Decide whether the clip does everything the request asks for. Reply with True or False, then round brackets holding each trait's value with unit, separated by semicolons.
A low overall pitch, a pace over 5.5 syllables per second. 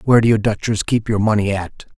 True (105 Hz; 6.3 syllables/s)